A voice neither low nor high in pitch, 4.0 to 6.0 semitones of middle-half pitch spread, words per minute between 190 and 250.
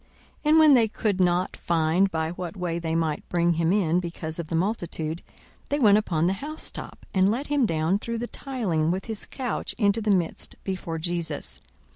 Yes: medium, 180 Hz; average, 4.9 semitones; average, 195 wpm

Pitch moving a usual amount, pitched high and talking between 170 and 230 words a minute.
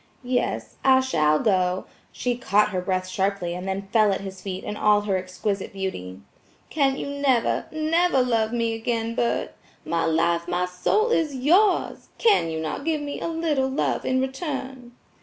No: wide, 6.3 semitones; high, 225 Hz; average, 175 wpm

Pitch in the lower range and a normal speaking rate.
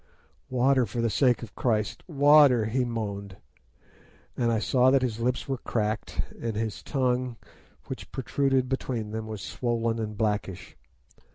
Yes: low, 120 Hz; average, 150 wpm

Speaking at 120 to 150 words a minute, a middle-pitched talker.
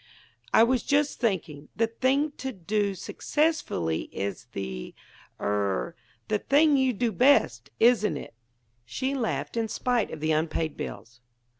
No: average, 140 wpm; high, 215 Hz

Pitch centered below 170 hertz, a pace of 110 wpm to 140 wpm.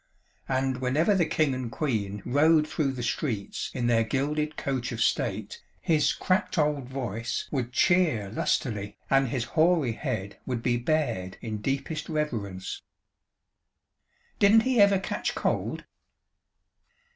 Yes: low, 135 Hz; slow, 135 wpm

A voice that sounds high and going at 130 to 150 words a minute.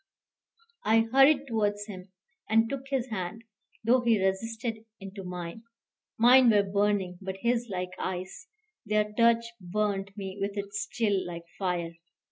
Yes: high, 205 Hz; average, 140 wpm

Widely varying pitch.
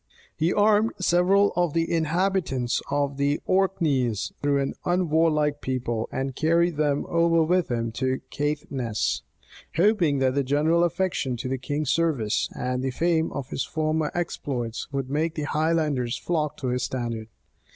No: average, 4.3 semitones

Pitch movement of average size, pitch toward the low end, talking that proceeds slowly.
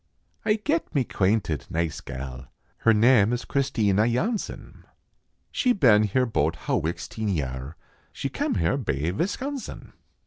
No: wide, 9.0 semitones; low, 110 Hz; slow, 130 wpm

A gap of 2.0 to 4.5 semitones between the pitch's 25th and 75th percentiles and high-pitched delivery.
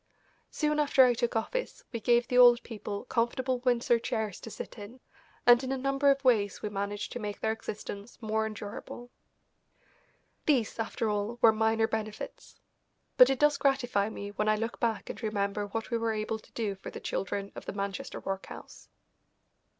Yes: average, 2.9 semitones; high, 225 Hz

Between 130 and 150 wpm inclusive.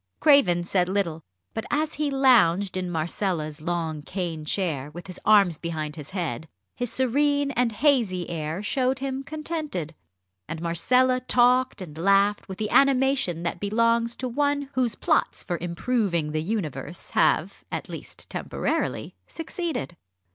Yes: average, 145 wpm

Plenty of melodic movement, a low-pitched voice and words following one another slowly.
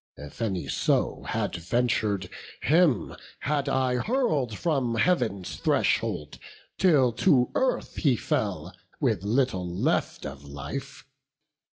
Yes: wide, 6.6 semitones; low, 120 Hz; slow, 110 wpm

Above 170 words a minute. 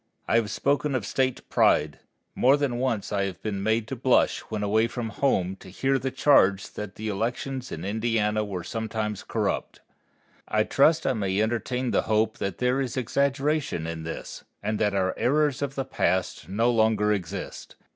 Yes: average, 180 wpm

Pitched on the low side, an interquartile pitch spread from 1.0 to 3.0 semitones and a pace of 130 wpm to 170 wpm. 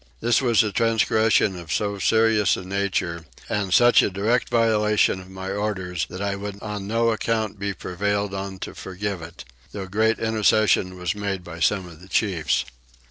No: low, 100 Hz; narrow, 2.5 semitones; average, 180 wpm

